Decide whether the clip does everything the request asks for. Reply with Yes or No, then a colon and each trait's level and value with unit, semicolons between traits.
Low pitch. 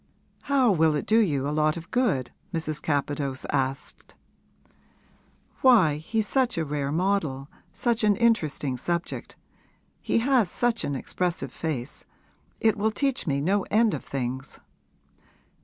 No: medium, 165 Hz